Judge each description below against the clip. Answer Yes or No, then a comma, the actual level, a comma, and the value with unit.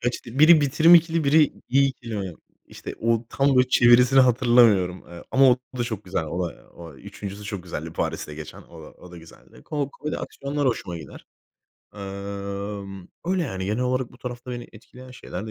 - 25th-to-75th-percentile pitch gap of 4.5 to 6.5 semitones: Yes, wide, 5.5 semitones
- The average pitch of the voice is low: Yes, low, 115 Hz